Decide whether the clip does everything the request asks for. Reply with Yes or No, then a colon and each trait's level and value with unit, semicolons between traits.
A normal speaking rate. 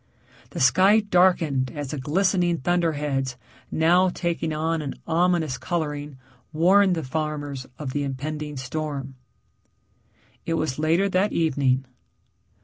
No: slow, 120 wpm